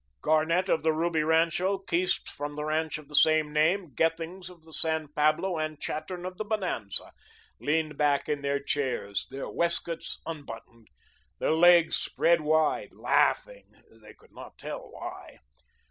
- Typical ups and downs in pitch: No, narrow, 2.3 semitones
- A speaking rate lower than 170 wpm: Yes, average, 160 wpm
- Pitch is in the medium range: Yes, medium, 160 Hz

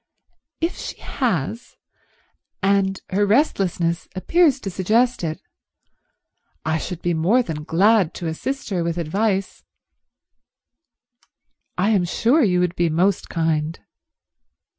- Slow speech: Yes, slow, 120 wpm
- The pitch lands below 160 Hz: No, medium, 185 Hz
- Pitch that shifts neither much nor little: Yes, average, 4.8 semitones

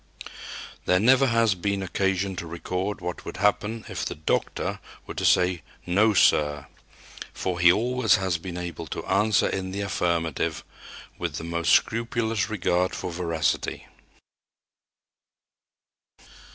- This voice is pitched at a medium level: No, very low, 95 Hz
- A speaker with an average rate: No, slow, 130 wpm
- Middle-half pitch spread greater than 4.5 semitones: No, average, 3.3 semitones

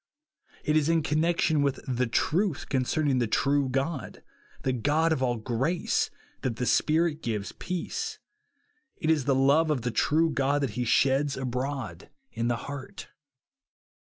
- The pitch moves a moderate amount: Yes, average, 3.7 semitones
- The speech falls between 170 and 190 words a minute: No, average, 160 wpm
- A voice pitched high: No, medium, 140 Hz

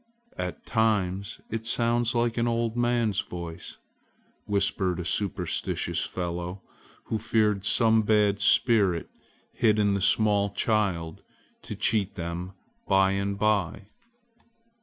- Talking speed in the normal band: No, slow, 115 wpm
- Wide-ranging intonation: No, average, 2.8 semitones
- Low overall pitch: Yes, low, 105 Hz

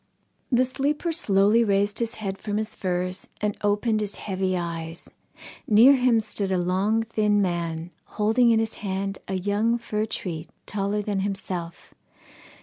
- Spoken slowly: No, average, 150 wpm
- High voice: Yes, high, 205 Hz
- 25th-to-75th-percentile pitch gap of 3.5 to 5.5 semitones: No, average, 2.9 semitones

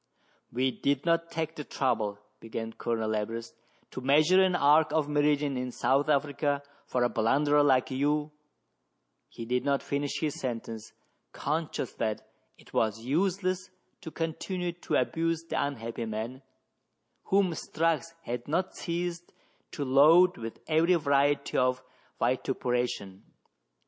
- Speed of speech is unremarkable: Yes, average, 145 wpm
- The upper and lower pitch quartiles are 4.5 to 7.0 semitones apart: Yes, average, 4.8 semitones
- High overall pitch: No, medium, 140 Hz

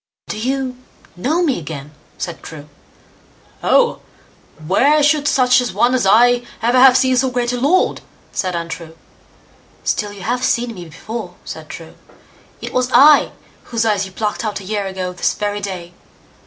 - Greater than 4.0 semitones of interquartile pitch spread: Yes, average, 5.2 semitones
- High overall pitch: Yes, high, 230 Hz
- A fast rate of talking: No, average, 170 wpm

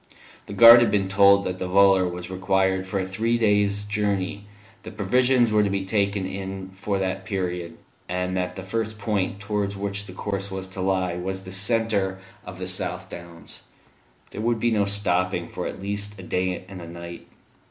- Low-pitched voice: Yes, very low, 95 Hz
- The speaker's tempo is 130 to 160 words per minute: No, average, 195 wpm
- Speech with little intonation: Yes, narrow, 1.7 semitones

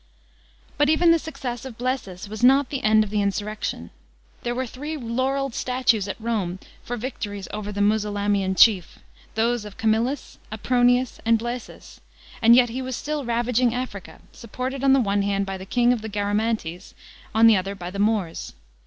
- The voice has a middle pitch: No, high, 225 Hz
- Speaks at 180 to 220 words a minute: Yes, average, 190 wpm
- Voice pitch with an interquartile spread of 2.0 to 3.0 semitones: No, average, 3.7 semitones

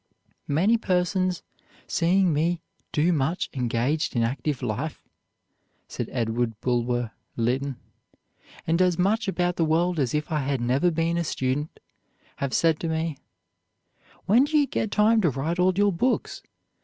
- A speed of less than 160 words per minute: Yes, average, 150 wpm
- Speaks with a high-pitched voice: No, medium, 160 Hz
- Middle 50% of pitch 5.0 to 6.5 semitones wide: Yes, average, 5.3 semitones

